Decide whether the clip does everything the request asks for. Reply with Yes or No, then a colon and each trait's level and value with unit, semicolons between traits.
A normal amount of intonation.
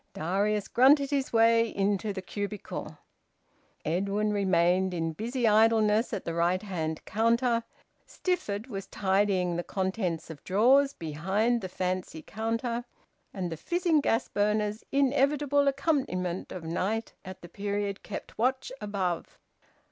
Yes: average, 4.1 semitones